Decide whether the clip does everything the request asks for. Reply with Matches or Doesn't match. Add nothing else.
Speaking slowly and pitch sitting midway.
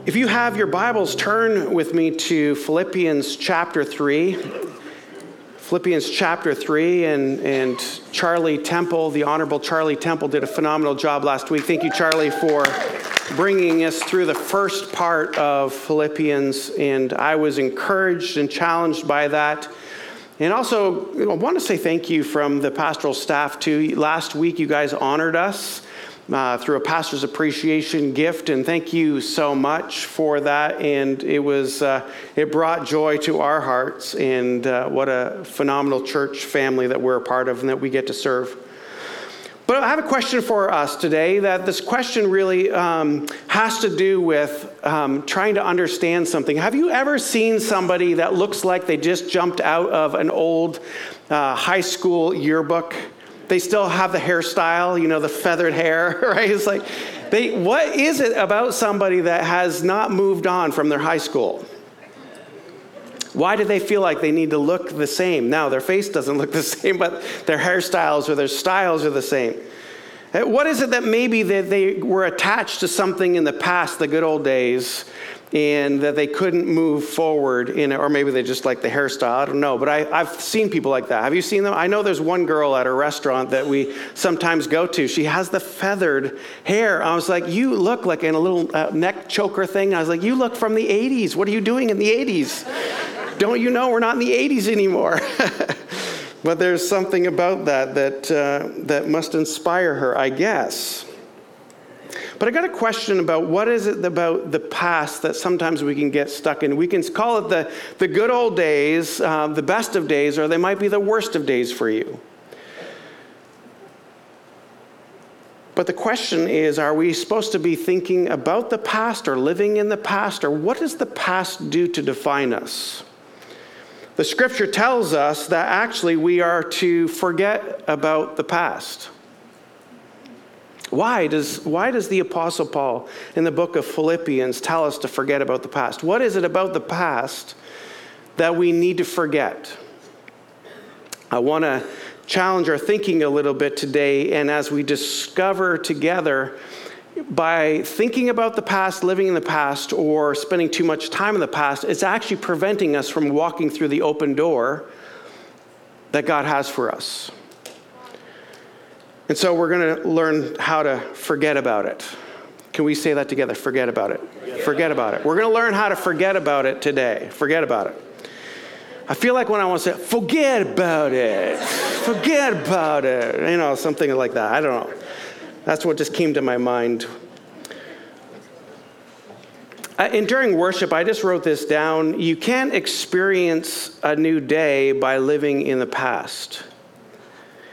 Doesn't match